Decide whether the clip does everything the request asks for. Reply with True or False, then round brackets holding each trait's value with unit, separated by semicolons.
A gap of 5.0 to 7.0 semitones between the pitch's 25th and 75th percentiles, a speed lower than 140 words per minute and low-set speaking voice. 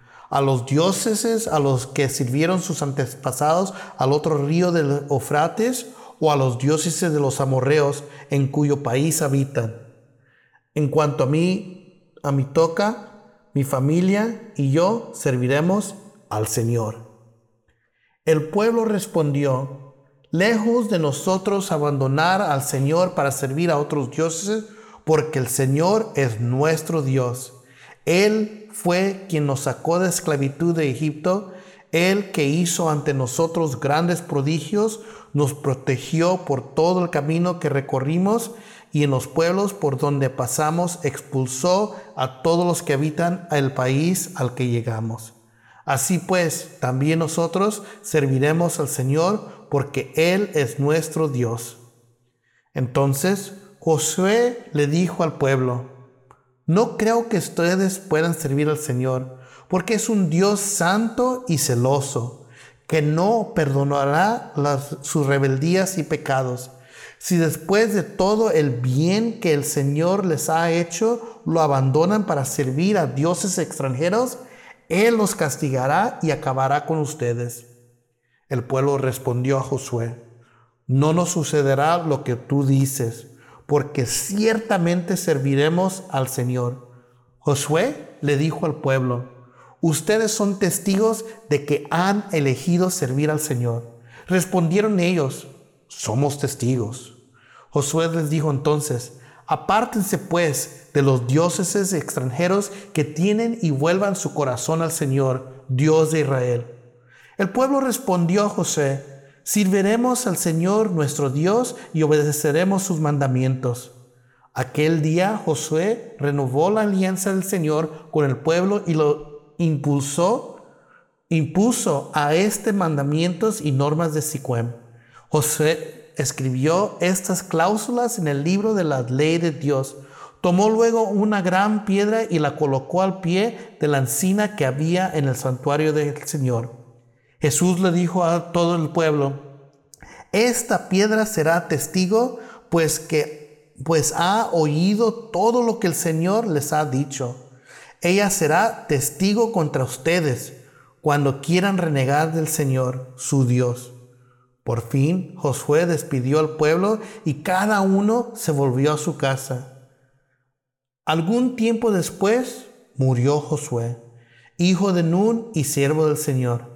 False (5.3 semitones; 130 wpm; 155 Hz)